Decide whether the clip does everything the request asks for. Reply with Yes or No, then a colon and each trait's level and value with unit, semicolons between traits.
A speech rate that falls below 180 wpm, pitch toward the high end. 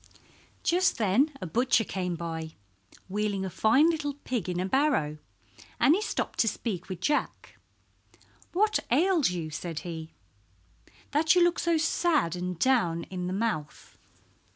Yes: average, 150 wpm; high, 210 Hz